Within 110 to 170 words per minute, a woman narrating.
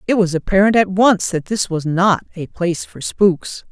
No: fast, 210 wpm; female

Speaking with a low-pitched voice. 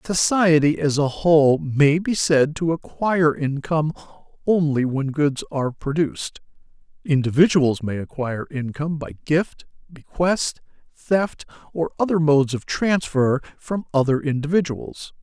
No: medium, 150 Hz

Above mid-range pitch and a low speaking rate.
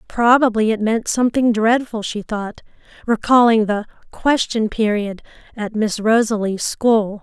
Yes: high, 220 Hz; slow, 125 wpm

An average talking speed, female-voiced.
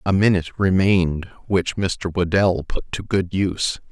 No: average, 155 wpm; male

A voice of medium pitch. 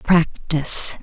Yes: medium, 165 Hz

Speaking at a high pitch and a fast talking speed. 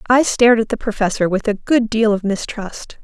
Yes: high, 220 Hz; fast, 220 wpm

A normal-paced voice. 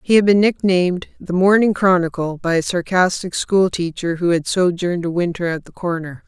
Yes: average, 180 wpm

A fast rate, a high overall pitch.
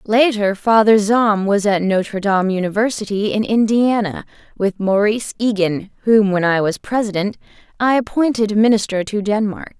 No: average, 140 wpm; high, 210 Hz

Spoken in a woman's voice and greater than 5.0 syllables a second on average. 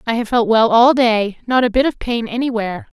Yes: female; 5.6 syllables/s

